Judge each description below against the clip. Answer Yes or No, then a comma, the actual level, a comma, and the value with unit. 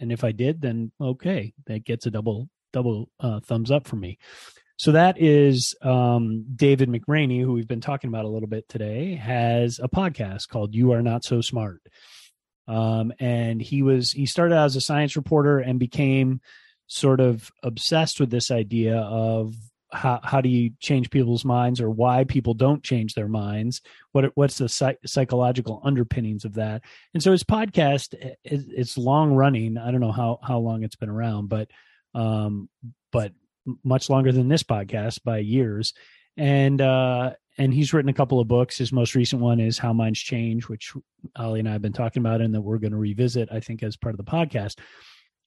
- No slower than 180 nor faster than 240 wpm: Yes, average, 195 wpm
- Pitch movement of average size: Yes, average, 3.0 semitones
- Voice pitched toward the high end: No, low, 125 Hz